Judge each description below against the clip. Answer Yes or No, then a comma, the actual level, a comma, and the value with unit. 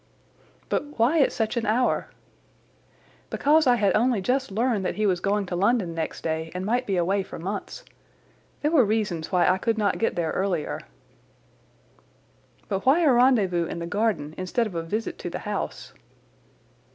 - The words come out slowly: No, average, 175 wpm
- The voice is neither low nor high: No, high, 205 Hz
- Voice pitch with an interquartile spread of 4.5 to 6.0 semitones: Yes, average, 5.0 semitones